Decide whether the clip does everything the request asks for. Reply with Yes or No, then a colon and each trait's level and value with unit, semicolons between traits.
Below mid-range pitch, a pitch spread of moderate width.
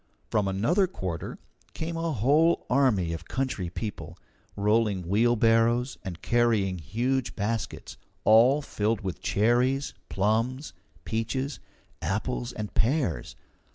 Yes: low, 115 Hz; average, 4.5 semitones